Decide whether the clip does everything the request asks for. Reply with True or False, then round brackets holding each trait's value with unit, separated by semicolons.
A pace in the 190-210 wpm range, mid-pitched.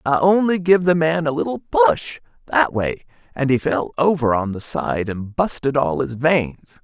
False (175 wpm; 145 Hz)